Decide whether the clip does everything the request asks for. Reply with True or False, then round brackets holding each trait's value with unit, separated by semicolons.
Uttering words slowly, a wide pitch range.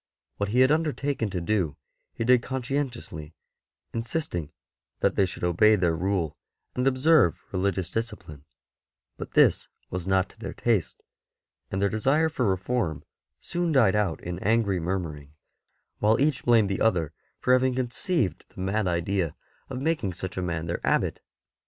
False (160 wpm; 6.1 semitones)